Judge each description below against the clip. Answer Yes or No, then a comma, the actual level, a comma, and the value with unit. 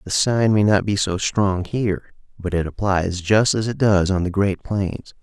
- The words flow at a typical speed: No, fast, 220 wpm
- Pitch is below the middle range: Yes, low, 100 Hz